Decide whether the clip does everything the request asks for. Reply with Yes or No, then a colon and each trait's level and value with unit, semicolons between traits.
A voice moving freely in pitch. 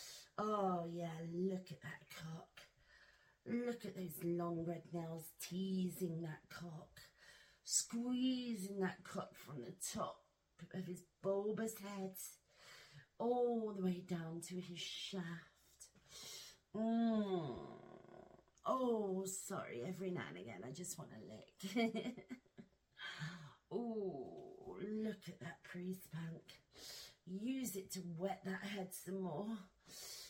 No: average, 3.4 semitones